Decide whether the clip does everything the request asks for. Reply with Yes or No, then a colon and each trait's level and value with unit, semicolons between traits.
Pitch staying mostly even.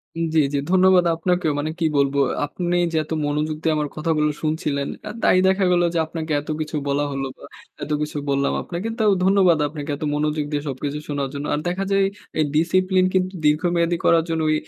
No: average, 3.3 semitones